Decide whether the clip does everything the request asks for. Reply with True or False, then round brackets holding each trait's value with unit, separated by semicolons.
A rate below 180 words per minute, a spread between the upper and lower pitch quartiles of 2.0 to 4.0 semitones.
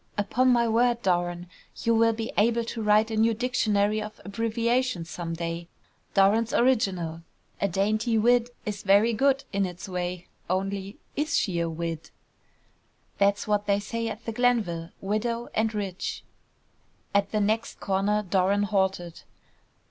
True (150 wpm; 3.2 semitones)